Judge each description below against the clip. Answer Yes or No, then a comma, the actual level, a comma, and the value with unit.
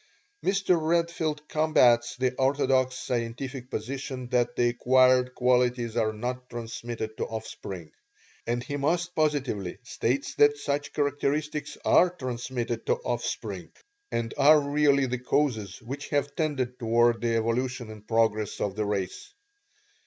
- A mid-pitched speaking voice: No, low, 125 Hz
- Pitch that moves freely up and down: No, average, 3.5 semitones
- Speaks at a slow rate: Yes, slow, 130 wpm